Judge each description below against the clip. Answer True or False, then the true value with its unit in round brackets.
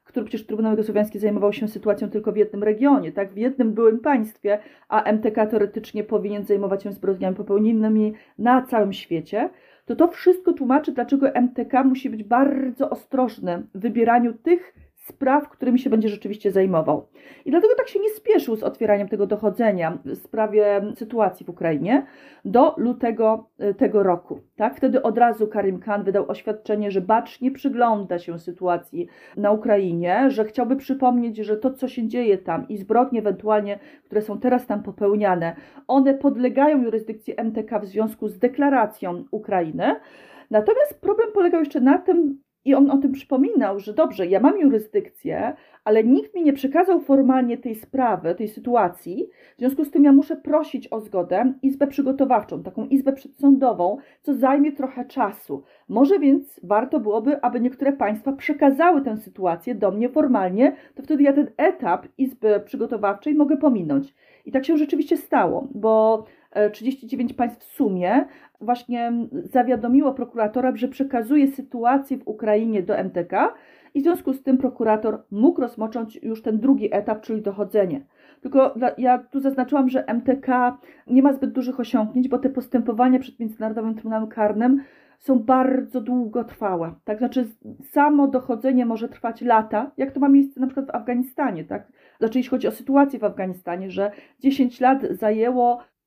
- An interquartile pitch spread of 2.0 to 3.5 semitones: False (4.3 semitones)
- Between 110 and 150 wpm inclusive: False (160 wpm)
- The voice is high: True (245 Hz)